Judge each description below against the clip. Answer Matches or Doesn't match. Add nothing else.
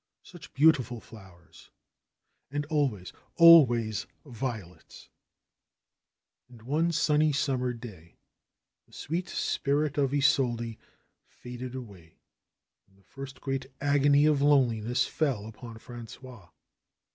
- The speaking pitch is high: Doesn't match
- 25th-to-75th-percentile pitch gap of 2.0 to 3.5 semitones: Doesn't match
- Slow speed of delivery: Matches